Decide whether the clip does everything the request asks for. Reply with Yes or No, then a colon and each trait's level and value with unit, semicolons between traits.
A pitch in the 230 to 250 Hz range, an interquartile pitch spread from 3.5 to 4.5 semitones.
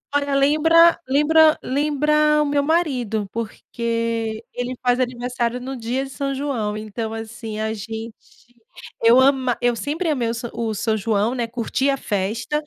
Yes: high, 245 Hz; average, 4.0 semitones